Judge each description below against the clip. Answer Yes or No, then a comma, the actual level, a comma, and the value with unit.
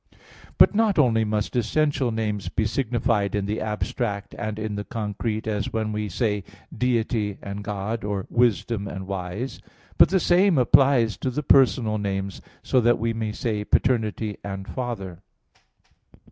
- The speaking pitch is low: Yes, low, 110 Hz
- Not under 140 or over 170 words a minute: Yes, average, 155 wpm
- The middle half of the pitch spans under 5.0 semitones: Yes, average, 2.8 semitones